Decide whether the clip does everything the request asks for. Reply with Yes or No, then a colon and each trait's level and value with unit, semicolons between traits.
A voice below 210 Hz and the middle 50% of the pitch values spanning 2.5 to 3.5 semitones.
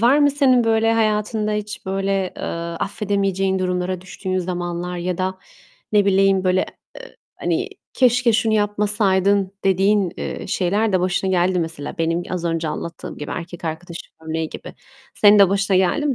Yes: high, 190 Hz; average, 2.8 semitones